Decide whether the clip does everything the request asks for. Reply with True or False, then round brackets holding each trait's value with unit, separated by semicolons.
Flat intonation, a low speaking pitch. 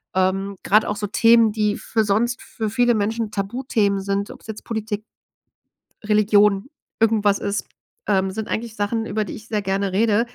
False (2.0 semitones; 210 Hz)